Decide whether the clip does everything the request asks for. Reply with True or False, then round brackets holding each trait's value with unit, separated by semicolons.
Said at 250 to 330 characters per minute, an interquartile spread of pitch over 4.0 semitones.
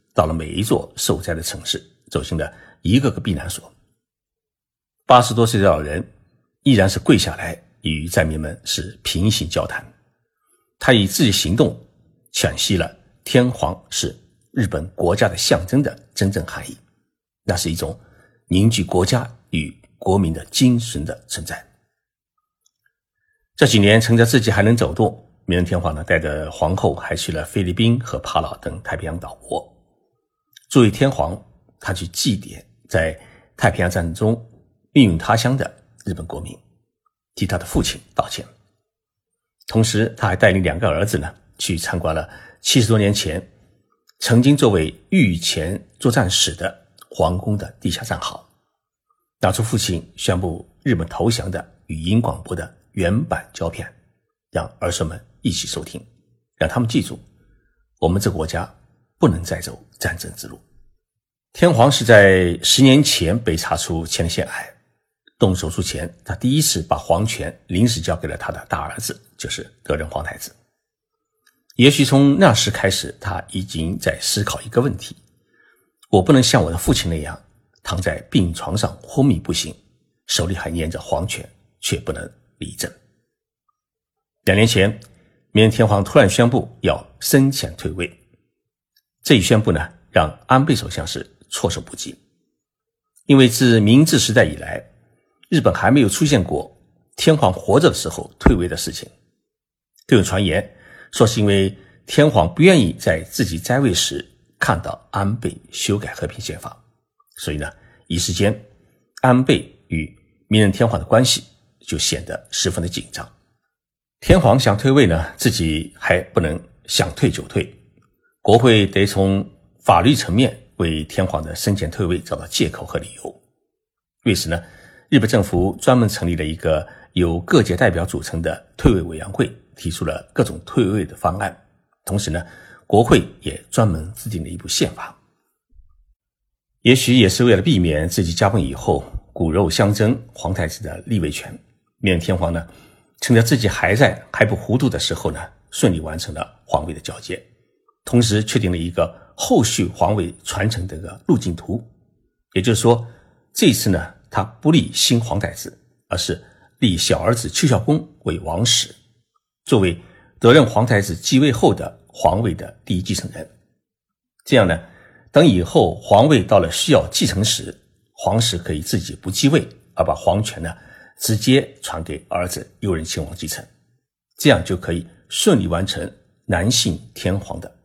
False (235 characters per minute; 5.4 semitones)